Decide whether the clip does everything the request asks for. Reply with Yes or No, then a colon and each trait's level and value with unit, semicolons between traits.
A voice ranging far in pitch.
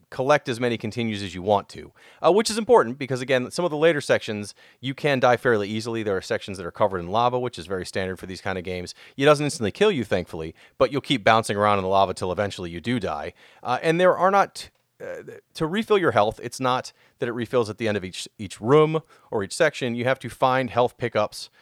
Yes: wide, 5.8 semitones